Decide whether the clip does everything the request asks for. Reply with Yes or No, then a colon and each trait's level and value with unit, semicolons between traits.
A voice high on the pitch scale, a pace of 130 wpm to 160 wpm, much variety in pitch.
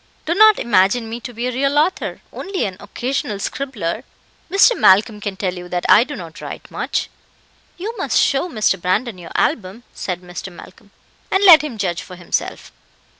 No: high, 220 Hz; average, 180 wpm; wide, 6.9 semitones